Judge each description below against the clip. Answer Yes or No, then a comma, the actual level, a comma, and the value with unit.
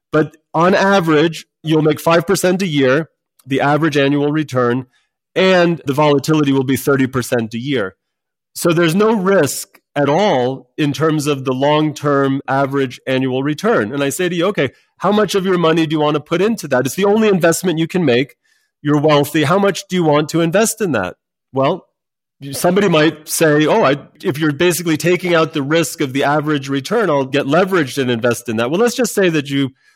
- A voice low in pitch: No, medium, 155 Hz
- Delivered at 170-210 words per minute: Yes, average, 200 wpm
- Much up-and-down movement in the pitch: No, average, 4.2 semitones